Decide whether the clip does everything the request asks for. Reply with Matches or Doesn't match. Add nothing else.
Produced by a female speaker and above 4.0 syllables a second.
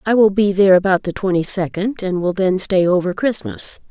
Matches